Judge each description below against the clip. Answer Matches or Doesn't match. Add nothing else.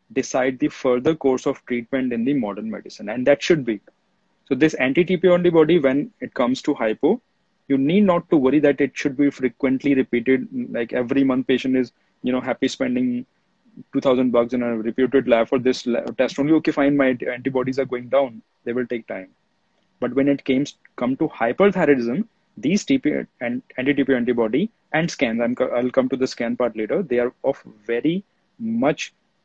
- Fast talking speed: Doesn't match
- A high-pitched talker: Doesn't match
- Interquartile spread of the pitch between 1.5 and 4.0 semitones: Doesn't match